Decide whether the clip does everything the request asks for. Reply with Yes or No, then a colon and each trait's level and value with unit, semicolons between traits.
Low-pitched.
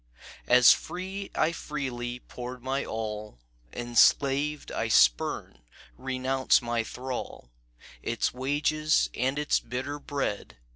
Yes: low, 130 Hz